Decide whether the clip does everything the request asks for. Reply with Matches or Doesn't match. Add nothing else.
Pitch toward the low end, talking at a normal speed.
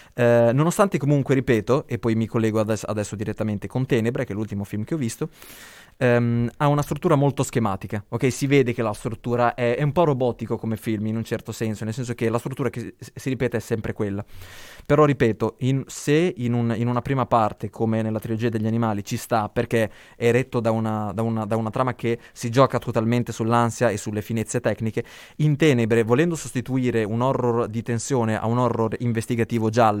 Doesn't match